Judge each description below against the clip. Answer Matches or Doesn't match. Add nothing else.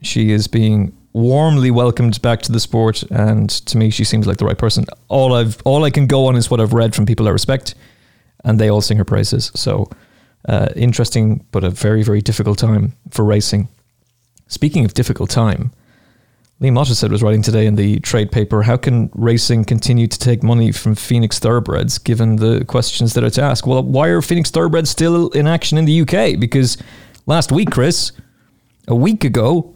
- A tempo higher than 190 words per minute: Matches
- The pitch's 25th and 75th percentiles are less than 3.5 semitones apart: Matches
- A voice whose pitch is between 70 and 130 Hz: Matches